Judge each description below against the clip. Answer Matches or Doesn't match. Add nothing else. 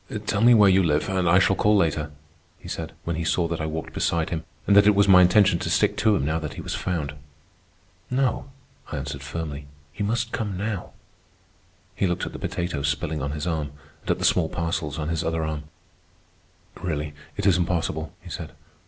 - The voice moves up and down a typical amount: Matches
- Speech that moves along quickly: Matches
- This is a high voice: Doesn't match